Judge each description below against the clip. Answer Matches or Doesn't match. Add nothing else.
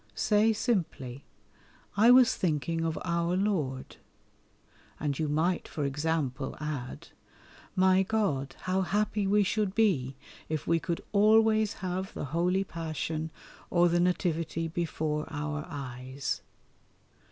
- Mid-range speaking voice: Matches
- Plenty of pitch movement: Doesn't match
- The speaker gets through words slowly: Matches